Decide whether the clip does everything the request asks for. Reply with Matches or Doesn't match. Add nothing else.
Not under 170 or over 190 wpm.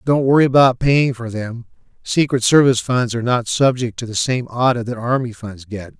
Doesn't match